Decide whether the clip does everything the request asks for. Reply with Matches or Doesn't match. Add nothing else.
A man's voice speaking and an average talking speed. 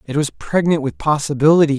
Matches